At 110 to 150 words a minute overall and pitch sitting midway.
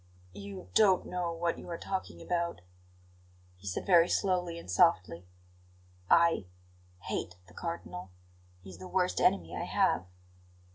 Yes: average, 140 wpm; medium, 165 Hz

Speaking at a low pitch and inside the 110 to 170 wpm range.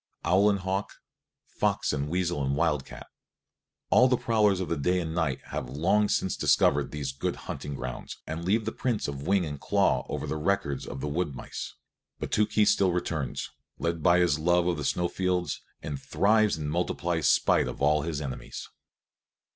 No: very low, 85 Hz; average, 185 wpm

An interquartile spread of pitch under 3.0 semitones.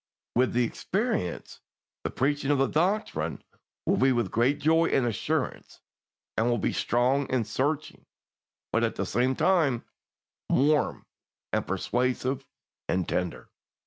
No: average, 3.6 semitones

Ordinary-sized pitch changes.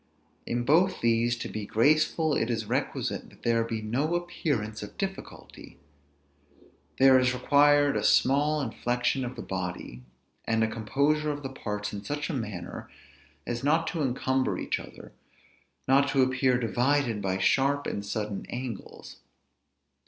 Yes: average, 4.4 semitones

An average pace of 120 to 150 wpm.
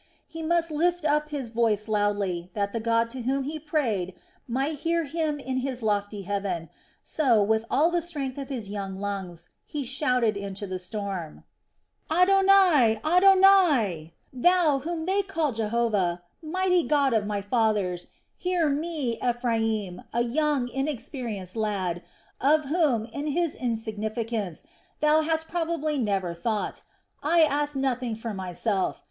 Yes: average, 140 wpm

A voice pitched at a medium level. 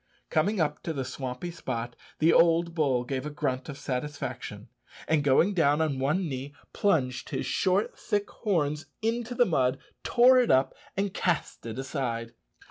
Yes: medium, 150 Hz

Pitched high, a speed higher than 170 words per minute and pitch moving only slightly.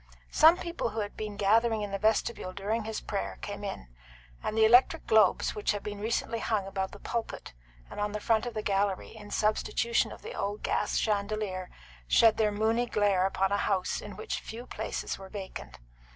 Yes: high, 210 Hz; average, 195 wpm; narrow, 1.9 semitones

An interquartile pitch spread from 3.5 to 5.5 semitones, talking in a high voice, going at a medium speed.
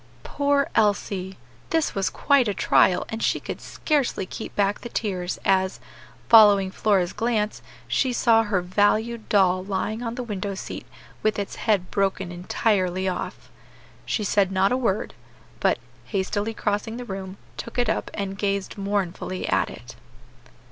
No: average, 2.9 semitones; high, 205 Hz; average, 155 wpm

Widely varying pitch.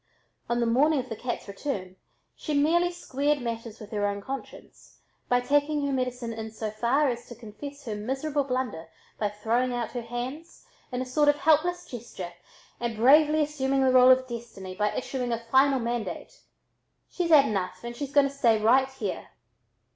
No: average, 3.9 semitones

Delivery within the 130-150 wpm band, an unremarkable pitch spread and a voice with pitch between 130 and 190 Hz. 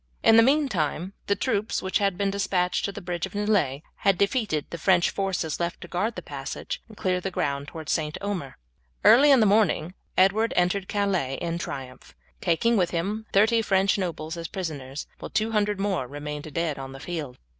No: average, 195 wpm; average, 4.6 semitones; medium, 185 Hz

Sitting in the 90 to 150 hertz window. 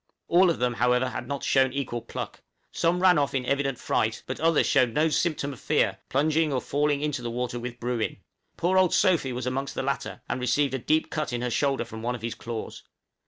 Yes: low, 135 Hz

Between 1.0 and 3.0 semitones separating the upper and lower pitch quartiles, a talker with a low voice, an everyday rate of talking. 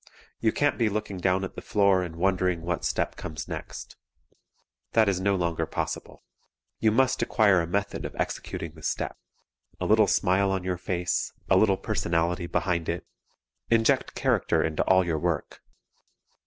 Yes: narrow, 2.6 semitones; very low, 95 Hz; average, 165 wpm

